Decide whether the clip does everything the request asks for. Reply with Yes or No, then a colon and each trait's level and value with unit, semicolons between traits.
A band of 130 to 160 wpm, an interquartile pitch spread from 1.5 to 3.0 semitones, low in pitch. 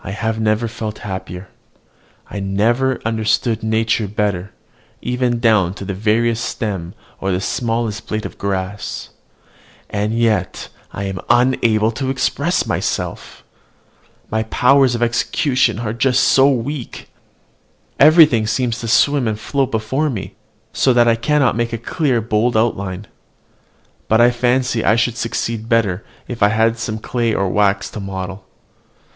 Yes: average, 140 wpm; narrow, 2.5 semitones; low, 115 Hz